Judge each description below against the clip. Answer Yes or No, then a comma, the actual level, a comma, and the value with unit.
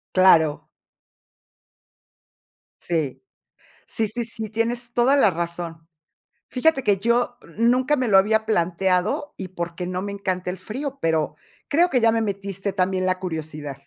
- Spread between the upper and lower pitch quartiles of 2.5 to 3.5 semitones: No, average, 4.9 semitones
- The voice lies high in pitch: Yes, high, 195 Hz